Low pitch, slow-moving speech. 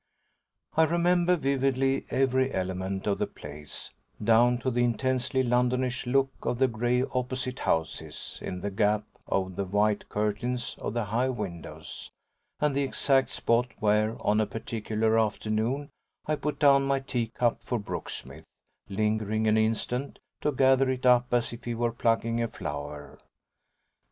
No: low, 120 Hz; average, 150 wpm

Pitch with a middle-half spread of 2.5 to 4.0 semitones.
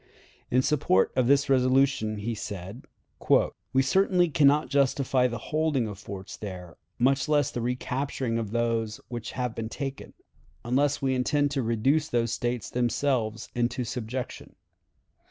Yes: average, 3.3 semitones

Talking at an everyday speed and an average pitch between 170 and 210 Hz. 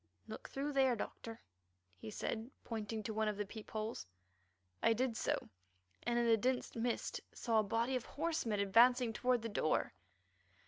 No: average, 170 wpm; high, 230 Hz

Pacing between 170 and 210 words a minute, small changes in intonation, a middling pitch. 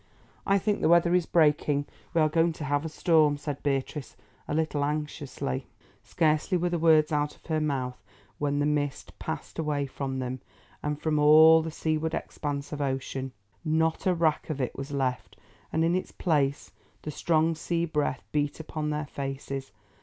Yes: average, 180 wpm; narrow, 2.2 semitones; medium, 150 Hz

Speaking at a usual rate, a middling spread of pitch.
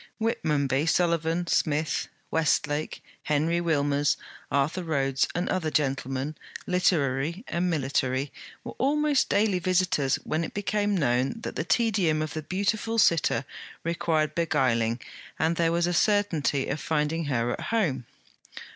No: slow, 130 wpm; average, 4.2 semitones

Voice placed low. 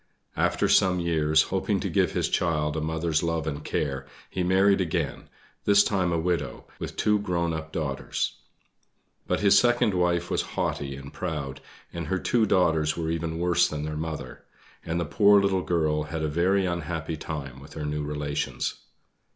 Yes: very low, 80 Hz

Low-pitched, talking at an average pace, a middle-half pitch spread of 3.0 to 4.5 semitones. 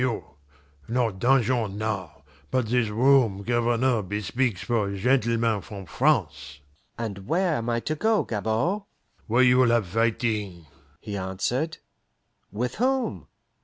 No: low, 115 Hz; slow, 125 wpm; average, 3.7 semitones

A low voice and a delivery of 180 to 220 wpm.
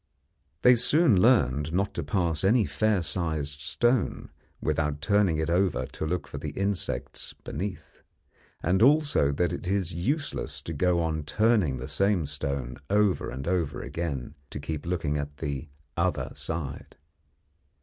No: very low, 85 Hz; average, 150 wpm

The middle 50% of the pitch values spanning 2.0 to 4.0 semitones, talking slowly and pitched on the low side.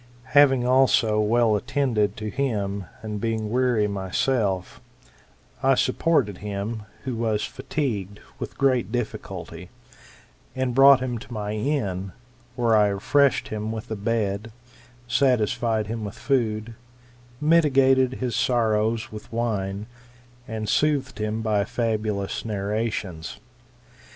Yes: average, 3.4 semitones; slow, 115 wpm; low, 110 Hz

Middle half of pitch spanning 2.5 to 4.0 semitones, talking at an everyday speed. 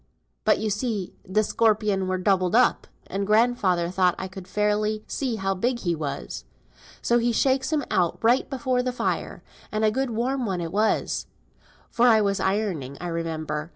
No: average, 4.4 semitones; average, 180 wpm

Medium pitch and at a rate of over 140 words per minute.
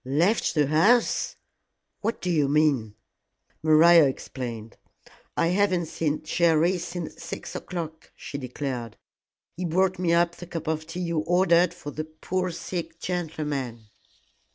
No: medium, 165 Hz; slow, 135 wpm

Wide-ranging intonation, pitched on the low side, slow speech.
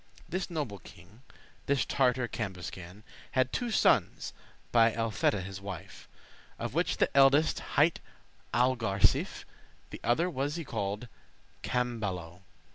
Yes: wide, 5.7 semitones; low, 115 Hz; slow, 120 wpm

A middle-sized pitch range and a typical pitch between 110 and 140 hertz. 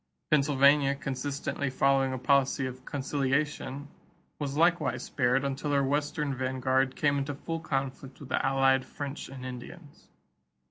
No: narrow, 1.5 semitones; low, 135 Hz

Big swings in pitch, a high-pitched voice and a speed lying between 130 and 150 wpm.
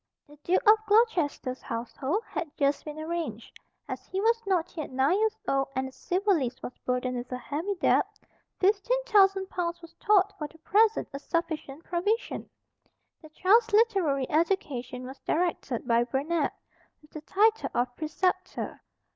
No: wide, 6.4 semitones; very high, 335 Hz; average, 160 wpm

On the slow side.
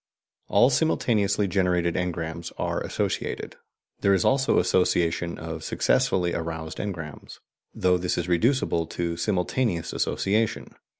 Yes: slow, 115 wpm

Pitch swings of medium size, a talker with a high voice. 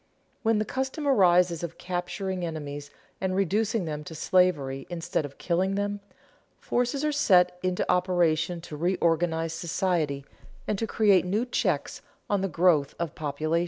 No: average, 3.3 semitones; medium, 180 Hz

